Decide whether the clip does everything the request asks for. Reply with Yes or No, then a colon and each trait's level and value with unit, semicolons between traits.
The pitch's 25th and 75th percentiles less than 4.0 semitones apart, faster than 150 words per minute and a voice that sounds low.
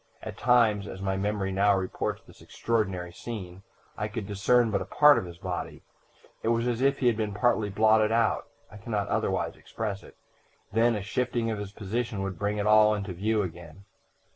Yes: average, 2.7 semitones; average, 200 wpm; low, 105 Hz